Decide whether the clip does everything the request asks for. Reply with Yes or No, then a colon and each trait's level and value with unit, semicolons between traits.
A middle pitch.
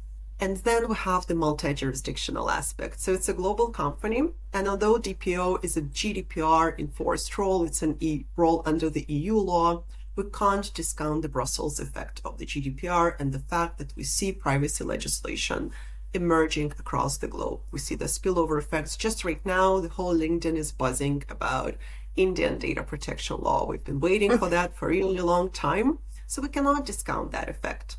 Yes: medium, 170 Hz